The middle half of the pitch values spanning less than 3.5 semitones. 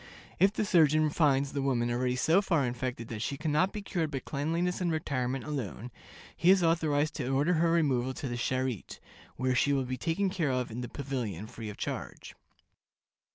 No: average, 4.5 semitones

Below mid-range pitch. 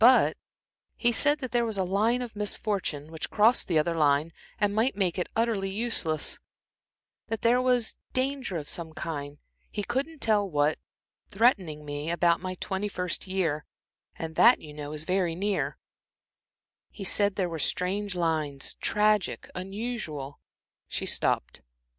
No: high, 190 Hz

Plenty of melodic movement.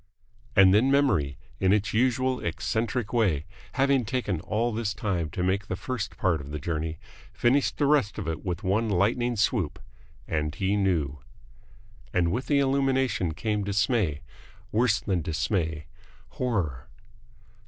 Yes: wide, 6.0 semitones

